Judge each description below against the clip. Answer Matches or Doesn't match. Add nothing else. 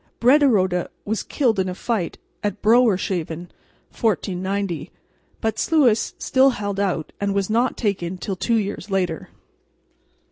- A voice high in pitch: Matches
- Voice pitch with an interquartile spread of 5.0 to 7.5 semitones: Doesn't match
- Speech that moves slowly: Matches